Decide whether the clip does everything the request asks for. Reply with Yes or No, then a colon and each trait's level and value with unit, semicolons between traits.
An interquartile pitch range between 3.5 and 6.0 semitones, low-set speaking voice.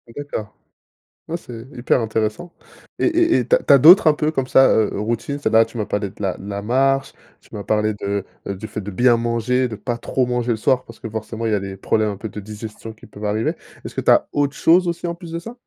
Yes: average, 4.6 semitones; low, 115 Hz